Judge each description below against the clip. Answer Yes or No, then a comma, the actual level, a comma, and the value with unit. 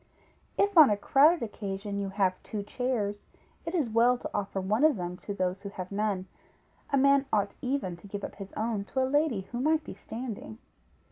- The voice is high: Yes, high, 215 Hz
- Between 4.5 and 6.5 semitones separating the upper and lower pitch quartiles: Yes, average, 5.1 semitones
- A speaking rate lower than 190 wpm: No, fast, 205 wpm